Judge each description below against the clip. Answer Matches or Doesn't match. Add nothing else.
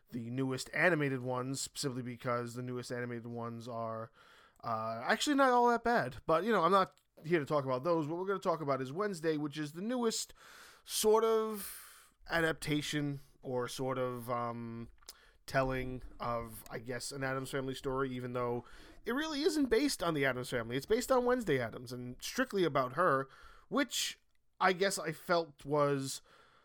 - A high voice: Doesn't match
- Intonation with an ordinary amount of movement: Doesn't match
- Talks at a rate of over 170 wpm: Matches